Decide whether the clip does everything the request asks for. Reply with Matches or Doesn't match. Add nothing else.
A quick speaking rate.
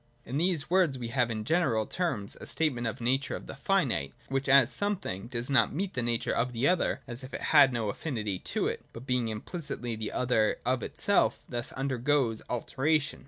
Matches